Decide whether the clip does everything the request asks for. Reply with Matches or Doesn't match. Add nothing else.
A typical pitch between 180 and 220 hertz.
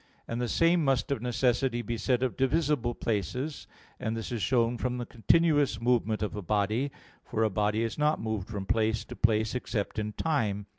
Doesn't match